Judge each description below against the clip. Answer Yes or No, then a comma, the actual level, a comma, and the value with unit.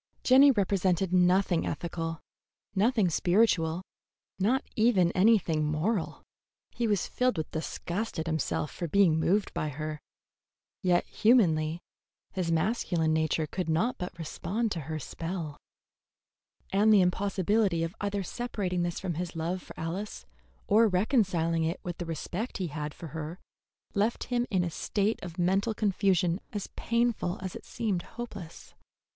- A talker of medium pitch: Yes, medium, 180 Hz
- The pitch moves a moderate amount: Yes, average, 4.0 semitones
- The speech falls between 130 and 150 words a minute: Yes, average, 145 wpm